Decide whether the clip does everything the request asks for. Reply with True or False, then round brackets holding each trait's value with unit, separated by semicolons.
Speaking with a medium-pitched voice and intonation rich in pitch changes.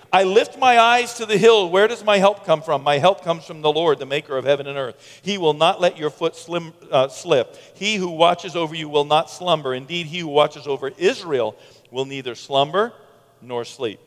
True (165 Hz; 5.7 semitones)